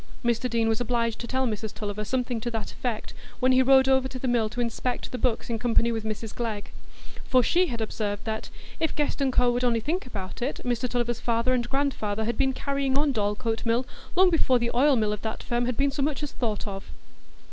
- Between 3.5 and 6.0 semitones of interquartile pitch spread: No, average, 2.7 semitones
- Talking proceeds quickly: Yes, fast, 230 wpm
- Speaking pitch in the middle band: No, high, 240 Hz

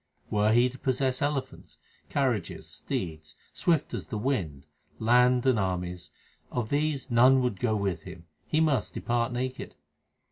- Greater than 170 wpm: No, average, 145 wpm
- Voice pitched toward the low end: Yes, low, 120 Hz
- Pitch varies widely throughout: No, average, 4.8 semitones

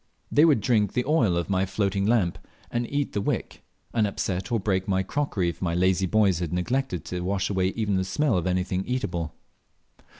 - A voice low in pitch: Yes, very low, 95 Hz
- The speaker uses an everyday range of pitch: Yes, average, 4.2 semitones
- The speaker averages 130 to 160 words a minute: No, average, 200 wpm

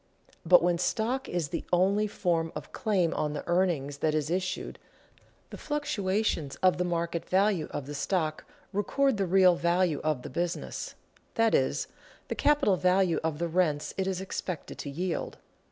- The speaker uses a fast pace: No, average, 170 wpm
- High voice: No, medium, 180 Hz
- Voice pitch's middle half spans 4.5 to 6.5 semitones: No, average, 3.1 semitones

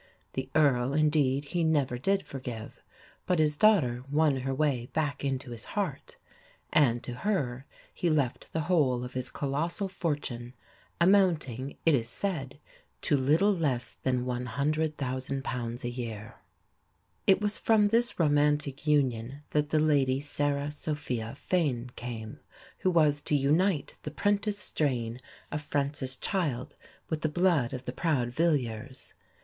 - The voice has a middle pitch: Yes, medium, 145 Hz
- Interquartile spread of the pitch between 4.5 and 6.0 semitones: No, average, 3.9 semitones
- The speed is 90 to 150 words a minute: Yes, average, 140 wpm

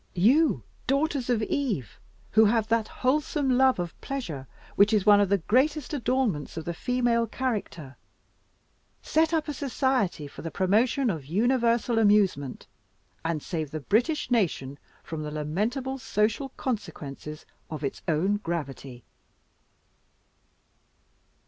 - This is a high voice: Yes, high, 215 Hz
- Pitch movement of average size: No, wide, 8.0 semitones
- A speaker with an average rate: No, slow, 130 wpm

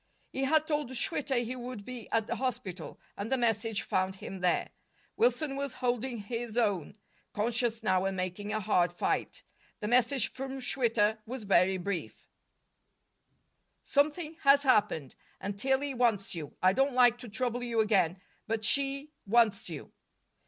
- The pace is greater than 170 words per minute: No, average, 155 wpm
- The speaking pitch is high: Yes, high, 230 Hz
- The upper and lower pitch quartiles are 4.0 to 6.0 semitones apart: Yes, average, 4.7 semitones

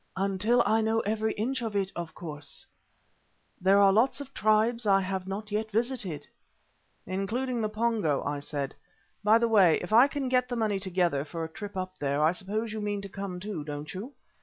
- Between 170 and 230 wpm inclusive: Yes, average, 200 wpm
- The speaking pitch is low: No, high, 205 Hz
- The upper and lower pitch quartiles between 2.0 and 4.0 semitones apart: Yes, average, 3.6 semitones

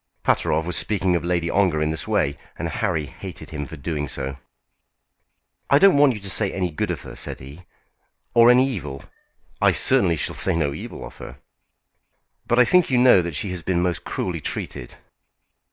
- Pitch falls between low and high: No, very low, 85 Hz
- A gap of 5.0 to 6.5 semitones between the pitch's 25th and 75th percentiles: Yes, wide, 5.5 semitones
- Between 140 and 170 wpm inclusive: No, average, 195 wpm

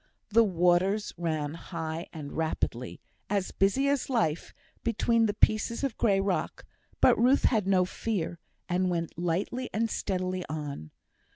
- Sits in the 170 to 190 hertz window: Yes, medium, 185 Hz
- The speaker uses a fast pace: No, average, 145 wpm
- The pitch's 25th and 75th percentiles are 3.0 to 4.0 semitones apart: No, average, 4.8 semitones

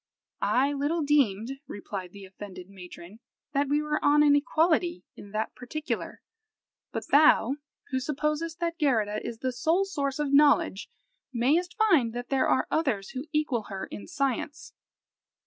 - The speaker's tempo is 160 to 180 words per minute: No, average, 150 wpm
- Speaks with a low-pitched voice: No, very high, 275 Hz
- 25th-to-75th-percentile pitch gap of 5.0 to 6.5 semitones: Yes, wide, 5.4 semitones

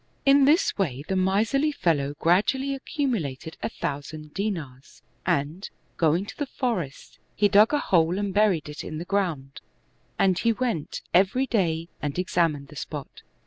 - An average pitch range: No, wide, 6.3 semitones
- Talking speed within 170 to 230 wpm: No, average, 155 wpm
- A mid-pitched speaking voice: Yes, medium, 180 Hz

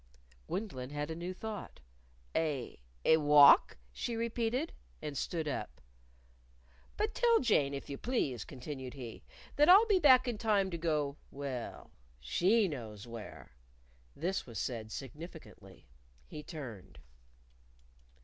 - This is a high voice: No, medium, 155 Hz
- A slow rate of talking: Yes, slow, 130 wpm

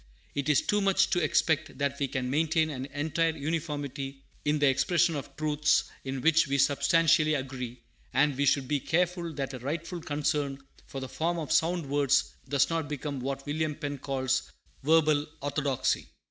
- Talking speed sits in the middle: Yes, average, 175 wpm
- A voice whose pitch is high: No, medium, 145 Hz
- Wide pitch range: No, average, 2.7 semitones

